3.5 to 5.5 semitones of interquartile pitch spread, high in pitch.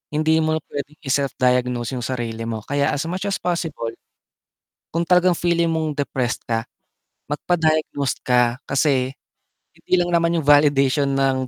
No: average, 4.1 semitones; medium, 145 Hz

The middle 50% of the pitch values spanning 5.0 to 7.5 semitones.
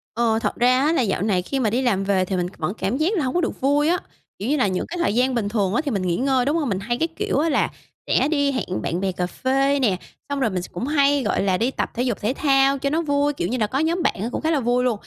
Yes: wide, 5.6 semitones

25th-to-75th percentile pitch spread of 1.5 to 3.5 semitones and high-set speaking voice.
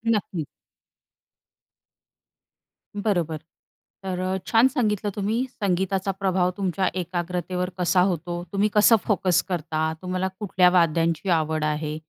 No: narrow, 2.5 semitones; medium, 180 Hz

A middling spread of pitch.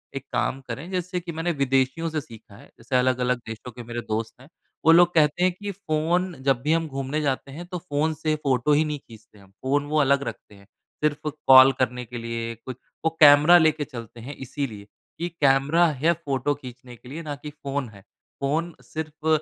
Yes: average, 4.1 semitones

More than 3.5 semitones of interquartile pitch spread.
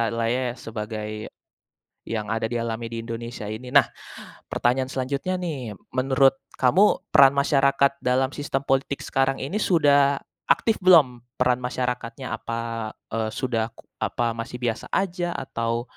No: average, 3.1 semitones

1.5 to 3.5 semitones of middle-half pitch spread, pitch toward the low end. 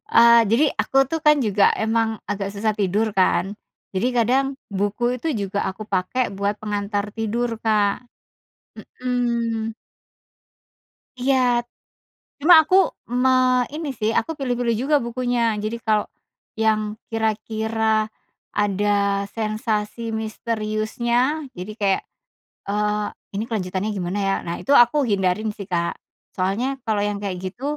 No: average, 2.7 semitones; high, 215 Hz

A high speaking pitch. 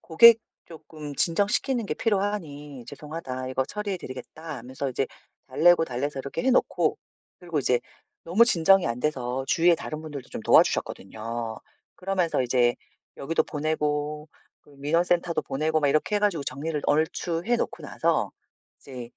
No: medium, 155 Hz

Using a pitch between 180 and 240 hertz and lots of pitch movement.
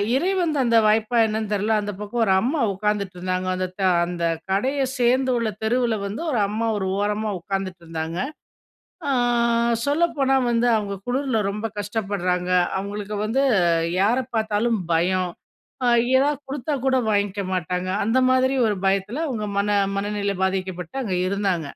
No: high, 210 Hz; average, 4.1 semitones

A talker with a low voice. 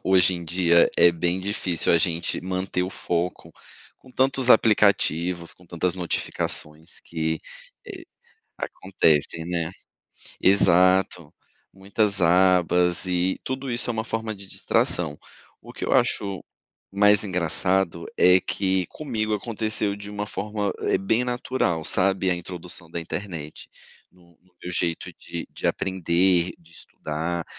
Yes: very low, 90 Hz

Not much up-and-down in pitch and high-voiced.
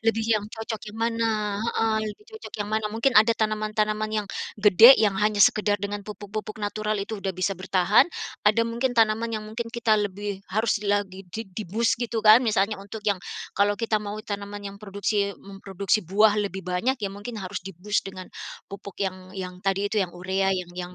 Yes: narrow, 1.9 semitones; high, 210 Hz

